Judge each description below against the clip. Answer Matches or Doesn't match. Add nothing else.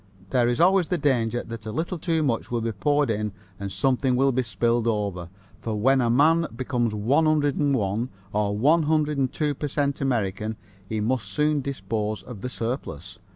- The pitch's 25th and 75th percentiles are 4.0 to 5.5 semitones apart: Matches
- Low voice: Matches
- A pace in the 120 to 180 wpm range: Matches